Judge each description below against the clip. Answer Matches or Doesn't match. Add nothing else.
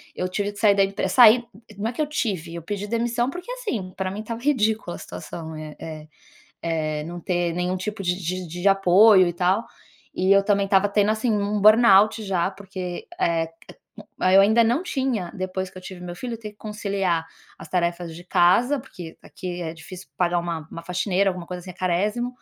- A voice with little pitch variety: Doesn't match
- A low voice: Doesn't match